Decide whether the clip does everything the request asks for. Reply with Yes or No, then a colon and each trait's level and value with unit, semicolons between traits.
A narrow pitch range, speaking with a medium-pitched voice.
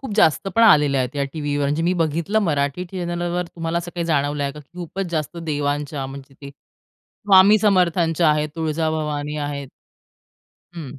No: average, 3.2 semitones; medium, 155 Hz